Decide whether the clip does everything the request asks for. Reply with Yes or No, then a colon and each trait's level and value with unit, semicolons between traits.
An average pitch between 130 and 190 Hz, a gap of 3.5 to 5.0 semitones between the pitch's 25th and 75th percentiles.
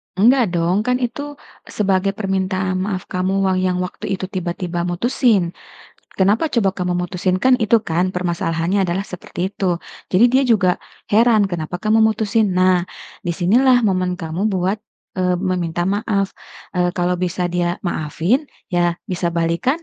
No: medium, 185 Hz; average, 2.9 semitones